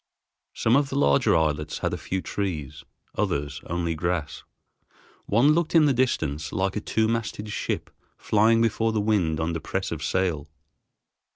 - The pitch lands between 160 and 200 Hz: No, very low, 95 Hz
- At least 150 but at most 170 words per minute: Yes, average, 160 wpm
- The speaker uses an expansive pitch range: Yes, wide, 6.2 semitones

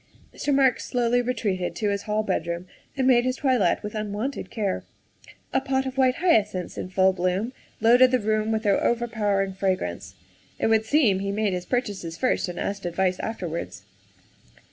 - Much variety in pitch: No, average, 4.6 semitones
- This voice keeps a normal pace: Yes, average, 190 wpm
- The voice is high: Yes, high, 215 Hz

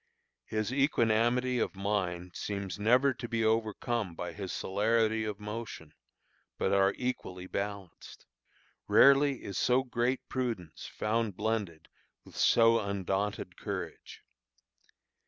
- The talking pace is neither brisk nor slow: No, slow, 115 wpm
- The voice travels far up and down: No, average, 3.3 semitones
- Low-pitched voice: Yes, low, 110 Hz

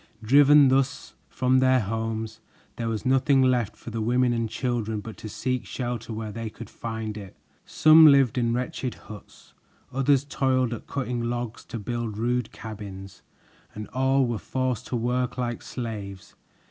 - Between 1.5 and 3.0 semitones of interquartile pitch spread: Yes, narrow, 2.6 semitones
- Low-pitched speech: Yes, low, 120 Hz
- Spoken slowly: No, average, 160 wpm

